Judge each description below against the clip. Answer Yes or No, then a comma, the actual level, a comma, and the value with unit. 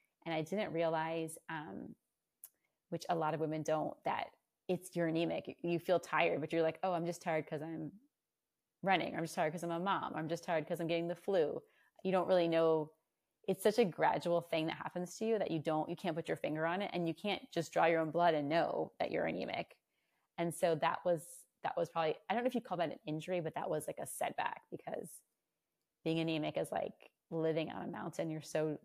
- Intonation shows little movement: Yes, narrow, 1.7 semitones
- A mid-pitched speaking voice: Yes, medium, 165 Hz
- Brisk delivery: Yes, fast, 235 wpm